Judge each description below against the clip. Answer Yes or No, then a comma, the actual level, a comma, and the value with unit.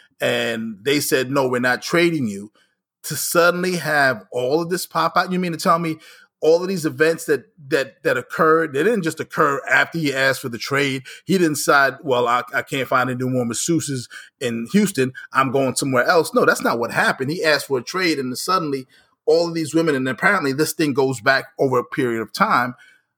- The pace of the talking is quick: Yes, fast, 210 wpm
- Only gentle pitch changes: No, average, 4.4 semitones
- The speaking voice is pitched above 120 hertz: Yes, medium, 140 Hz